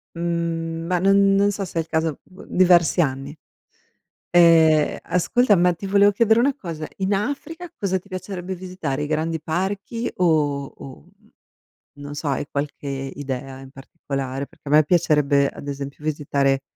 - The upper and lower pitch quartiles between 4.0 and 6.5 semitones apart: Yes, average, 4.9 semitones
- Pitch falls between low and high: Yes, medium, 165 Hz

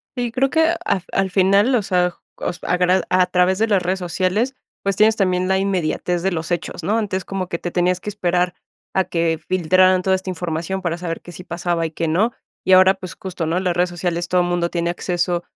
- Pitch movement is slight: Yes, narrow, 1.6 semitones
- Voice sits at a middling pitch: Yes, medium, 180 Hz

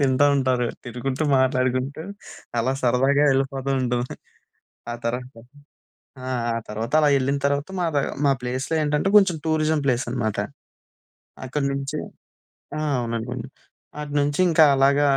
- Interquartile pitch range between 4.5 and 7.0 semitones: No, narrow, 2.5 semitones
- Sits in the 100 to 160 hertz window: Yes, low, 135 Hz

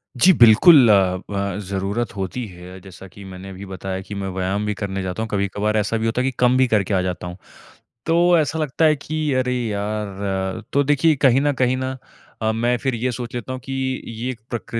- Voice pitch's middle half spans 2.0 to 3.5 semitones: No, average, 4.6 semitones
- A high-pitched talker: No, low, 110 Hz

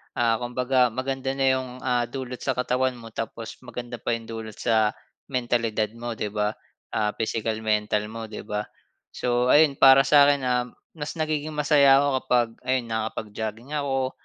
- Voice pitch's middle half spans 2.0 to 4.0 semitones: Yes, average, 3.0 semitones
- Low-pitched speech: Yes, low, 125 Hz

